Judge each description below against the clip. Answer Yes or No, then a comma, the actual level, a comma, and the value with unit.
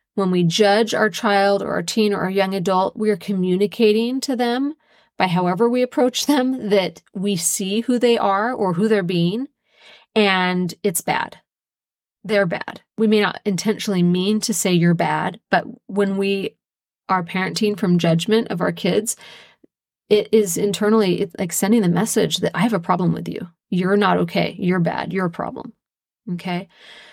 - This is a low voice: No, high, 200 Hz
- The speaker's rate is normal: Yes, average, 175 wpm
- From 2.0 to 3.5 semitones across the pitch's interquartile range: Yes, average, 3.0 semitones